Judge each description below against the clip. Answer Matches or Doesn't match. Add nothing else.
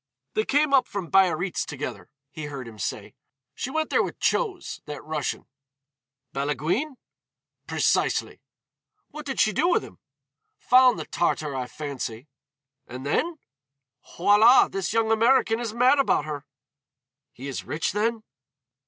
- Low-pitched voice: Doesn't match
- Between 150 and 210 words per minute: Doesn't match